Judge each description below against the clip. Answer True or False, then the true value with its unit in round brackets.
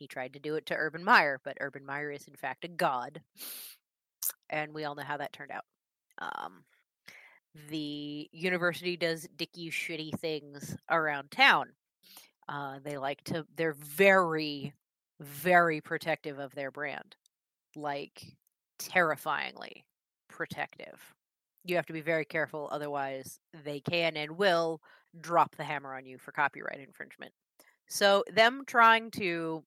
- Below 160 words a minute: True (140 wpm)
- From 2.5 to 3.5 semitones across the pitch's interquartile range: True (2.8 semitones)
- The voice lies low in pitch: False (155 Hz)